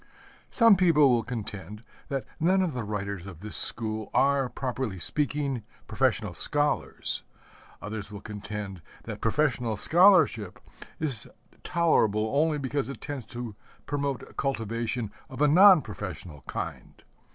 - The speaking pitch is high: No, low, 125 Hz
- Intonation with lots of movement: Yes, wide, 5.7 semitones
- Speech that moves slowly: Yes, slow, 130 wpm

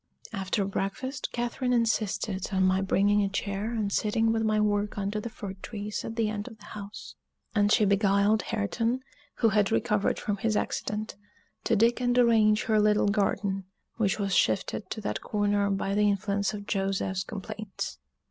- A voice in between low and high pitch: No, high, 210 Hz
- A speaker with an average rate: Yes, average, 175 wpm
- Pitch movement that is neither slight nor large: No, narrow, 1.9 semitones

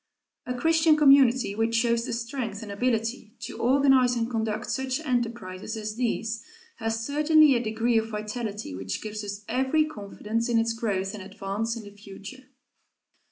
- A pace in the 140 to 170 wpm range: Yes, average, 160 wpm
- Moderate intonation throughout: Yes, average, 3.2 semitones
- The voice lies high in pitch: Yes, high, 230 Hz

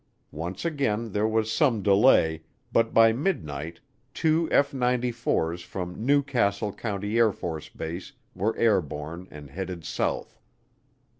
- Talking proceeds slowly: Yes, slow, 120 wpm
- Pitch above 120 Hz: No, low, 105 Hz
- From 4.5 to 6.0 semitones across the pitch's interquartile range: Yes, wide, 5.6 semitones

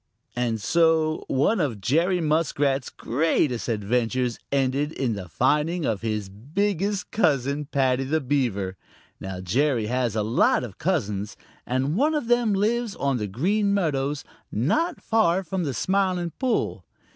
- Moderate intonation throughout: No, wide, 7.1 semitones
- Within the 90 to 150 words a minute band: Yes, average, 145 wpm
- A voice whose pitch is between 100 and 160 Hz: Yes, medium, 140 Hz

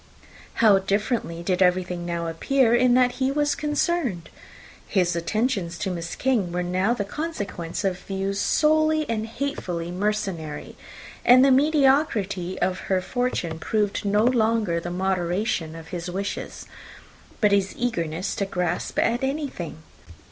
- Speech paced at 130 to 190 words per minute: Yes, average, 140 wpm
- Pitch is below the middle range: No, high, 200 Hz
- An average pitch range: No, wide, 5.9 semitones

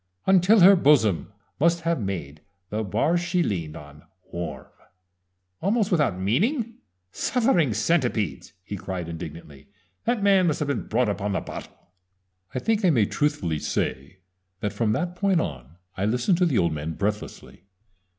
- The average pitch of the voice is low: Yes, low, 115 Hz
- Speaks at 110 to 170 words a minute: Yes, average, 160 wpm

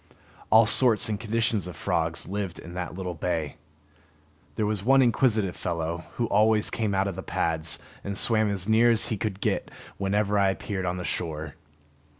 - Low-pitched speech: Yes, low, 100 Hz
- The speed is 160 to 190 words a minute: Yes, average, 180 wpm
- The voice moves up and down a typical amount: Yes, average, 3.8 semitones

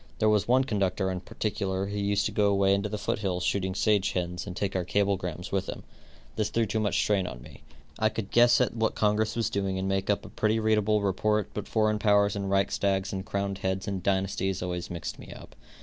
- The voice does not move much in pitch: Yes, narrow, 2.0 semitones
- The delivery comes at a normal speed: No, fast, 225 wpm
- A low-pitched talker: Yes, low, 100 Hz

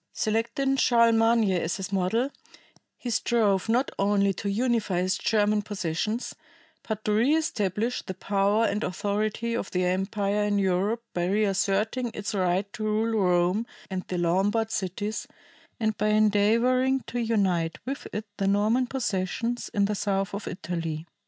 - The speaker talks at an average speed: Yes, average, 150 wpm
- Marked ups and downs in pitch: No, average, 3.0 semitones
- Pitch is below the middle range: No, high, 210 Hz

